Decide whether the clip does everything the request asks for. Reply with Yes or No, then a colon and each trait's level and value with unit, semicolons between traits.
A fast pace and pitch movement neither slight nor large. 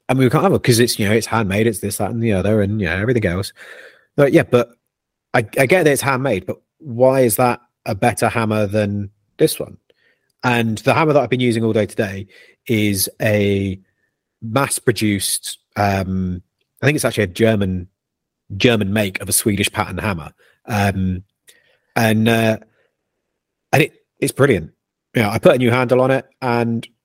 No: average, 195 wpm; average, 3.5 semitones